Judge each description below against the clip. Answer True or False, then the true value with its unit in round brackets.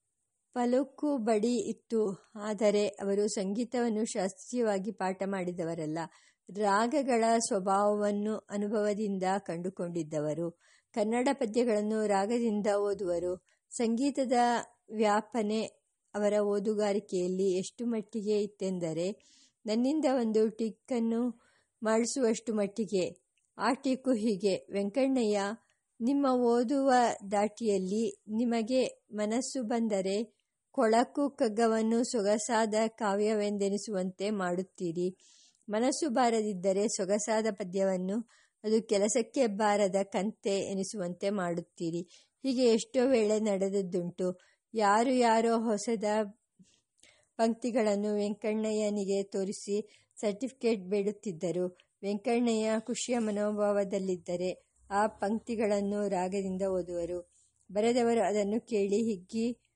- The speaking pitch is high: True (210 Hz)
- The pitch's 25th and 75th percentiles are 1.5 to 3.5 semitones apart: True (2.8 semitones)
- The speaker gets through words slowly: True (75 wpm)